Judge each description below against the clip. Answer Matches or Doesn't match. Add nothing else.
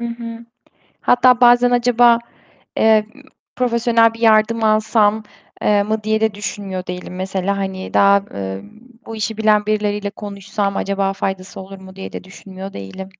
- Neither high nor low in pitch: Doesn't match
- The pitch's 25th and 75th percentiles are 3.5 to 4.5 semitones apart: Doesn't match